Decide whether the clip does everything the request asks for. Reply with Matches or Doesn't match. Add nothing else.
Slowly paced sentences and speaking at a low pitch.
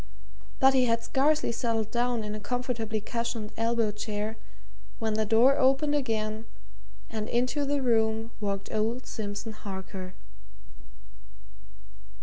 Doesn't match